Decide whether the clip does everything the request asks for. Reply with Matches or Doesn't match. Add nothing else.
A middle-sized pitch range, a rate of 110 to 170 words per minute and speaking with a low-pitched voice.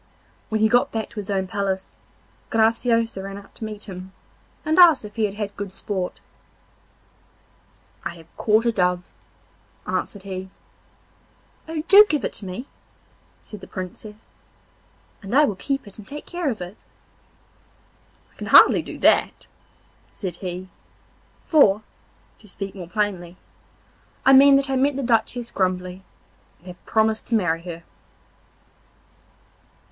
Doesn't match